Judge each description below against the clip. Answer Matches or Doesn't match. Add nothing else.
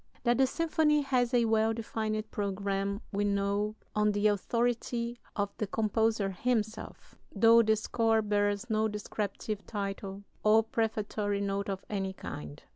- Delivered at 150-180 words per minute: Doesn't match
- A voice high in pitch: Matches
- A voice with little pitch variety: Matches